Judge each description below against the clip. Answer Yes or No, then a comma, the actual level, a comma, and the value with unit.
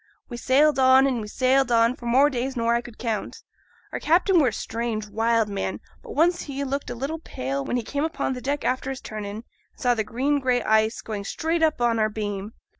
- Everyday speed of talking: No, fast, 230 wpm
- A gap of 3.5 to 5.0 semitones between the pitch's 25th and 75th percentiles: Yes, average, 3.9 semitones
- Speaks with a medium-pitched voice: No, high, 245 Hz